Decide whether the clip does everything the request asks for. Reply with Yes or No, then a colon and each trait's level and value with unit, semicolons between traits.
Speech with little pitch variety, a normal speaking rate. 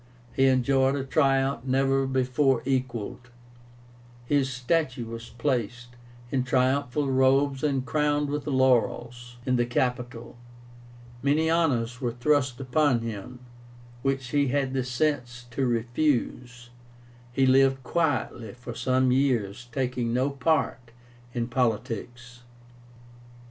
No: narrow, 2.1 semitones; slow, 115 wpm